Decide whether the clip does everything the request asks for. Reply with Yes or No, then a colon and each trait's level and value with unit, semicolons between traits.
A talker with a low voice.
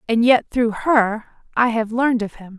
No: high, 230 Hz